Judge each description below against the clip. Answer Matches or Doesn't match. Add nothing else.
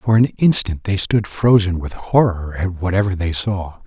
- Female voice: Doesn't match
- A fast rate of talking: Doesn't match